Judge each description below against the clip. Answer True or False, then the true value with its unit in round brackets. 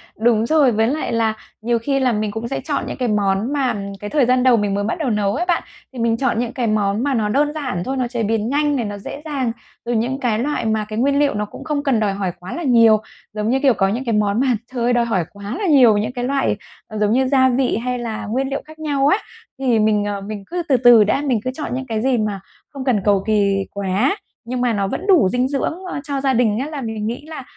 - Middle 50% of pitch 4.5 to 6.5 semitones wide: False (4.1 semitones)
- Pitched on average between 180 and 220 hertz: False (240 Hz)